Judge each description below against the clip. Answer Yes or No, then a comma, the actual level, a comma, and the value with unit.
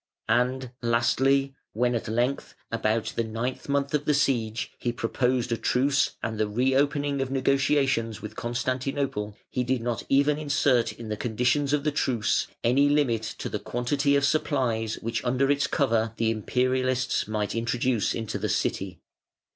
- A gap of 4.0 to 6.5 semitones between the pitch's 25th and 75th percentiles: No, average, 3.2 semitones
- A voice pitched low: Yes, low, 125 Hz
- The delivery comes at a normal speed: Yes, average, 160 wpm